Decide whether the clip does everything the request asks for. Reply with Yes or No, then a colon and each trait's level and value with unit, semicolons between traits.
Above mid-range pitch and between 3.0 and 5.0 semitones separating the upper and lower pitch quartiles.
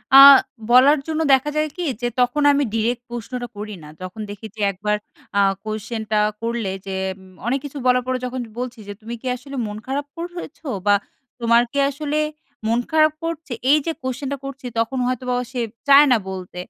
Yes: very high, 250 Hz; average, 4.3 semitones